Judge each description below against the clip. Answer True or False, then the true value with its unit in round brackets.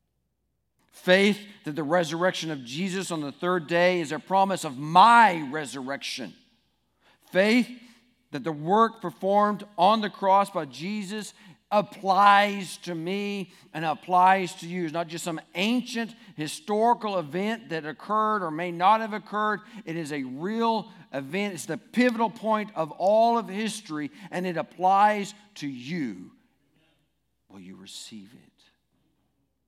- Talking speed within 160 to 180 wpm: False (140 wpm)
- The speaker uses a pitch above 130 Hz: True (185 Hz)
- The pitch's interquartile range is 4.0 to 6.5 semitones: True (4.3 semitones)